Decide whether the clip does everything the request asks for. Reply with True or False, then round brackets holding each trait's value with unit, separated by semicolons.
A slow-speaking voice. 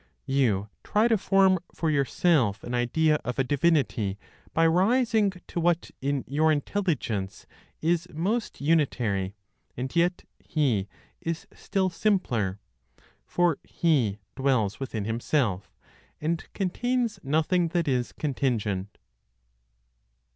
True (110 wpm)